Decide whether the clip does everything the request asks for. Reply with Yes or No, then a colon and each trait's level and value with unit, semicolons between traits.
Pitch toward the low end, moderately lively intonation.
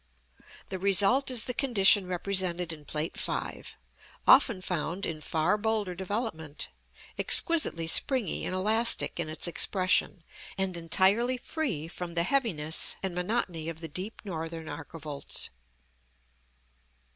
No: medium, 185 Hz; average, 4.7 semitones